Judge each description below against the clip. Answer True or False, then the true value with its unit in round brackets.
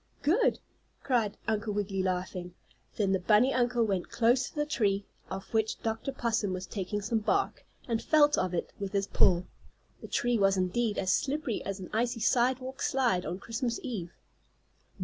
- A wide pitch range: False (4.2 semitones)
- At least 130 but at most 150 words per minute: False (170 wpm)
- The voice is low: False (220 Hz)